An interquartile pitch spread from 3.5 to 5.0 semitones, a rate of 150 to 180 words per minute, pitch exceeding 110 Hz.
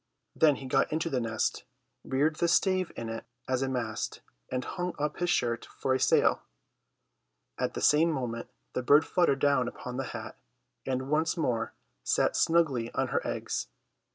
Yes: average, 4.4 semitones; average, 175 wpm; low, 135 Hz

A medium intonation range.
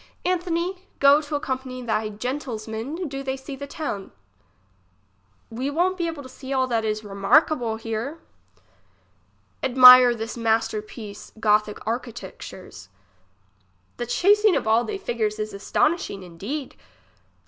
Yes: average, 5.0 semitones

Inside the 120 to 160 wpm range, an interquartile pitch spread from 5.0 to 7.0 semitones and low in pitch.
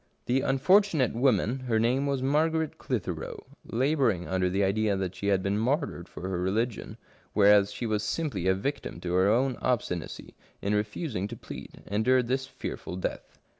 No: average, 175 wpm; wide, 5.4 semitones; low, 110 Hz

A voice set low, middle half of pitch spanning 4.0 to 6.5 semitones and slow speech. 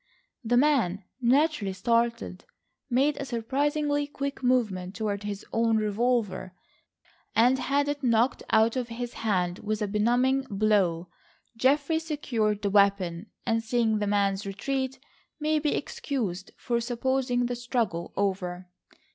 No: high, 230 Hz; average, 4.5 semitones; slow, 130 wpm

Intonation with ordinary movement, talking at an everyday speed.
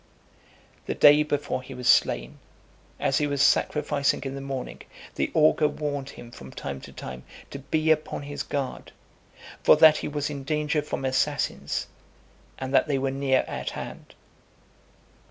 No: narrow, 2.1 semitones; average, 165 wpm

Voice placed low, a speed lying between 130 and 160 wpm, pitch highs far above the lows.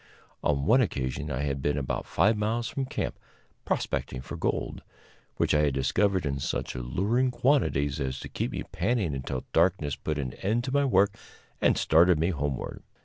No: very low, 80 Hz; average, 180 wpm; wide, 7.9 semitones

